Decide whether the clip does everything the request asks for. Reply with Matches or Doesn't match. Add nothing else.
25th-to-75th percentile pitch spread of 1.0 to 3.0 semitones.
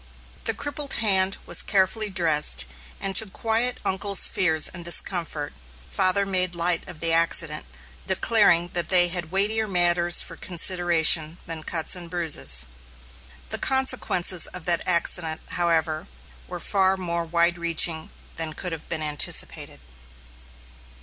Matches